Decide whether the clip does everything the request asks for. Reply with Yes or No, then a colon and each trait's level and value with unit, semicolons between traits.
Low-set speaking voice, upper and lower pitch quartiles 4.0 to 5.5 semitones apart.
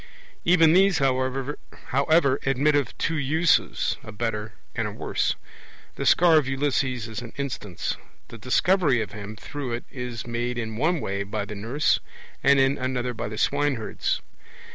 Yes: low, 130 Hz; average, 4.3 semitones